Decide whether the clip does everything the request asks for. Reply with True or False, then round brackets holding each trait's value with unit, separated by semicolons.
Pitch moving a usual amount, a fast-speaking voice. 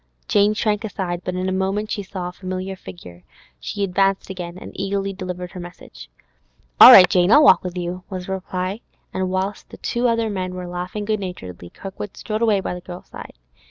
False (1.9 semitones; 210 wpm)